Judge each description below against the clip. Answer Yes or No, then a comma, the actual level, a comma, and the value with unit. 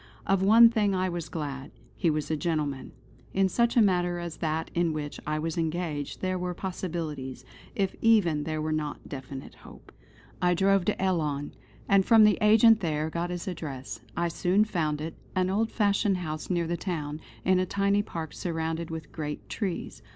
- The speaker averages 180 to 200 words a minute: Yes, average, 185 wpm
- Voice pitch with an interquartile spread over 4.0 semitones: No, average, 3.7 semitones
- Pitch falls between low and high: Yes, medium, 170 Hz